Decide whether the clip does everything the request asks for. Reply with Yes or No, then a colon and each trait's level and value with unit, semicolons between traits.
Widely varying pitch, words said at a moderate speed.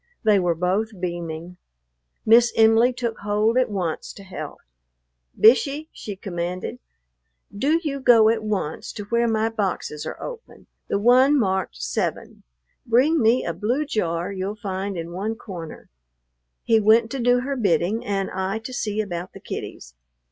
No: average, 4.1 semitones; average, 155 wpm